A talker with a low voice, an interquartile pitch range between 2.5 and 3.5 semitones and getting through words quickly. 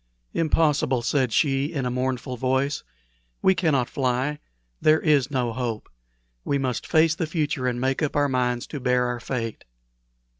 No: low, 130 Hz; average, 3.0 semitones; average, 160 wpm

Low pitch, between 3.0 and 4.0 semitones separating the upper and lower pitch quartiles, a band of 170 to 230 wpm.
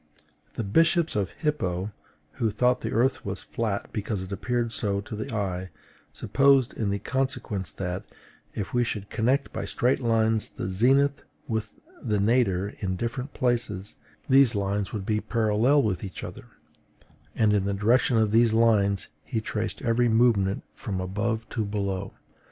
No: low, 110 Hz; average, 3.4 semitones; average, 155 wpm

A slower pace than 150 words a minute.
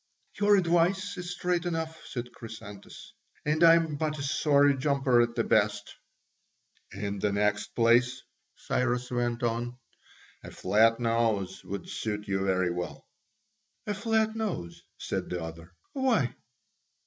Yes: slow, 135 wpm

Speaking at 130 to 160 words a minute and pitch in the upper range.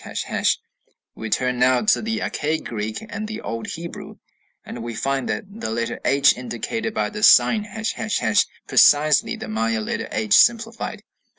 No: average, 150 wpm; medium, 140 Hz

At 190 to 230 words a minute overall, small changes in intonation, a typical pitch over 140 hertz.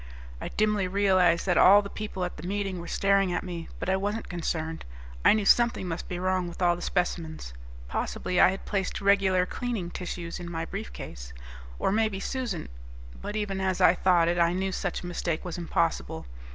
Yes: average, 195 wpm; narrow, 2.3 semitones; medium, 185 Hz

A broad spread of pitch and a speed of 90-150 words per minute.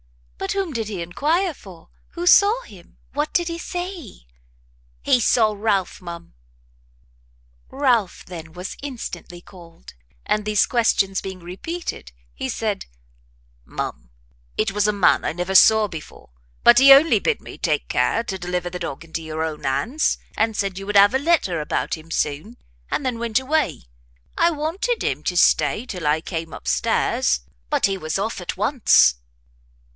No: wide, 7.6 semitones; average, 165 wpm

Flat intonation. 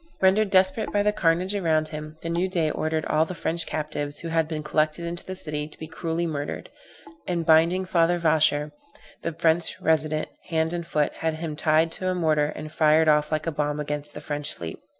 Yes: narrow, 1.9 semitones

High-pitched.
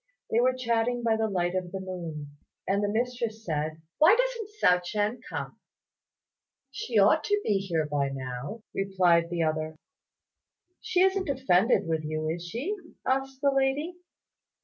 Yes: high, 205 Hz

